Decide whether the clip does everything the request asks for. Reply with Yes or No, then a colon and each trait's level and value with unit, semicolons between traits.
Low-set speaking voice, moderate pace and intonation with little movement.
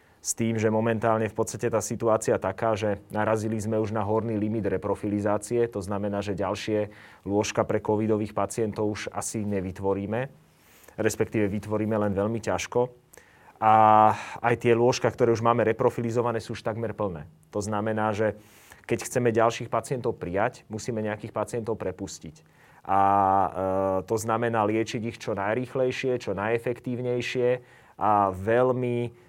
Yes: low, 110 Hz; average, 140 wpm; narrow, 2.0 semitones